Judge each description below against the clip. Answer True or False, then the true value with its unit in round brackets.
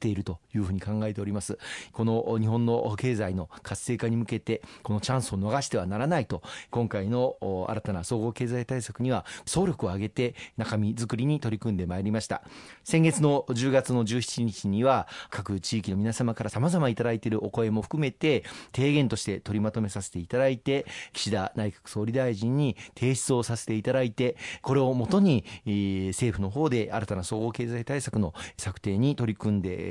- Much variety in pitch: False (3.4 semitones)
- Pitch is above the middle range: False (115 Hz)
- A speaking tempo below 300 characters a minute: False (335 characters per minute)